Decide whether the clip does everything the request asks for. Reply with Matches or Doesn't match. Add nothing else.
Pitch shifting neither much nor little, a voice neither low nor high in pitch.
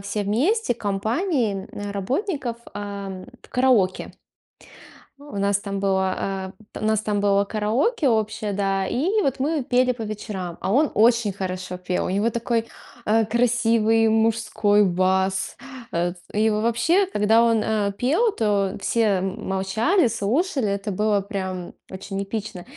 Doesn't match